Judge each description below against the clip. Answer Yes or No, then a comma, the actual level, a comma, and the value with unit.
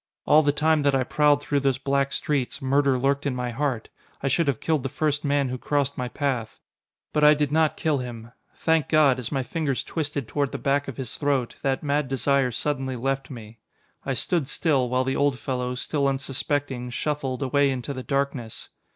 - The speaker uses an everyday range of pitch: No, narrow, 2.1 semitones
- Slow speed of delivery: No, fast, 205 wpm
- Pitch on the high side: No, medium, 140 Hz